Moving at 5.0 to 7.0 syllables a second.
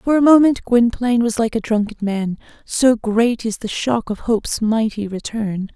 No: 4.7 syllables/s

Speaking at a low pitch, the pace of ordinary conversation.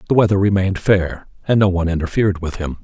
No: very low, 95 Hz; fast, 210 wpm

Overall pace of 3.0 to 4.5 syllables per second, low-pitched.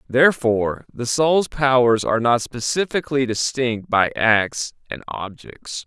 Yes: 4.3 syllables/s; low, 125 Hz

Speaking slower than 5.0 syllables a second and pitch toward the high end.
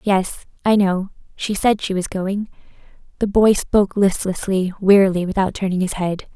Yes: 4.8 syllables/s; high, 195 Hz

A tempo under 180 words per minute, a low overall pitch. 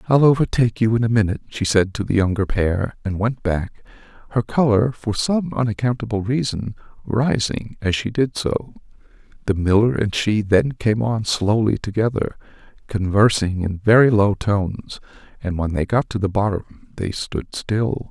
Yes: average, 165 wpm; low, 110 Hz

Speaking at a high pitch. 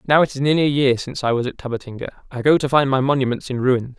No: low, 130 Hz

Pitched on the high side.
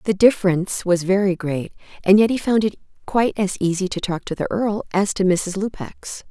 Yes: high, 195 Hz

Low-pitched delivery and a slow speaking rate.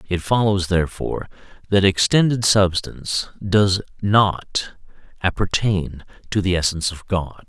Yes: very low, 95 Hz; slow, 110 wpm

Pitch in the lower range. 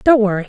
No: high, 220 Hz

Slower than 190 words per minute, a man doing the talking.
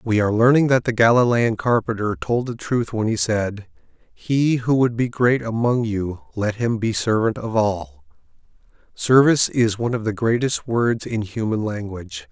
Yes: average, 175 wpm; male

